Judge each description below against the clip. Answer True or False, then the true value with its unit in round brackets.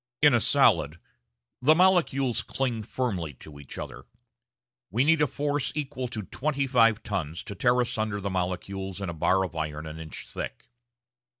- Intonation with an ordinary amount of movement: False (7.1 semitones)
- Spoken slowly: False (170 wpm)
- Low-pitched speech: True (110 Hz)